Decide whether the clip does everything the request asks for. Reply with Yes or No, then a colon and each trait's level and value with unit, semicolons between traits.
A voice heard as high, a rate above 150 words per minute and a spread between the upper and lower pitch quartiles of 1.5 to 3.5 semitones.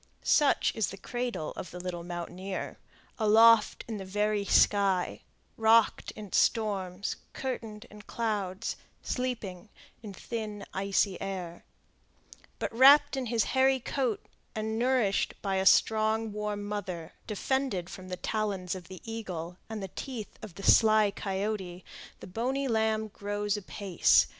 No: high, 210 Hz; average, 140 wpm; average, 2.9 semitones